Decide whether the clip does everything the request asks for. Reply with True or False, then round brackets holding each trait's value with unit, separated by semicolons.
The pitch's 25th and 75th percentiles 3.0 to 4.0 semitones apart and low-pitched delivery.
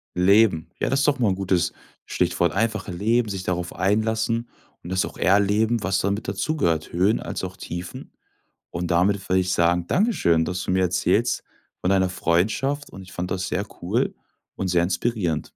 True (3.7 semitones; 95 Hz)